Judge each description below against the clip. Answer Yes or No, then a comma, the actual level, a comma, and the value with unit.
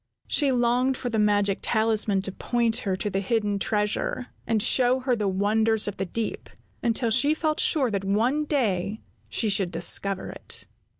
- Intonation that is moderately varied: Yes, average, 3.6 semitones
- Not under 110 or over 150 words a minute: No, average, 175 wpm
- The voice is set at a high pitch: Yes, high, 220 Hz